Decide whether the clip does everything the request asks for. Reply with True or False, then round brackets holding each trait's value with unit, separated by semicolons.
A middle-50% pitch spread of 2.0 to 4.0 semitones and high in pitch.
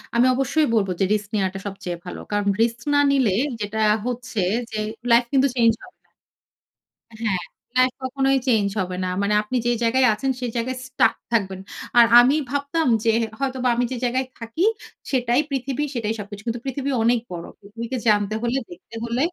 True (3.7 semitones; 235 Hz)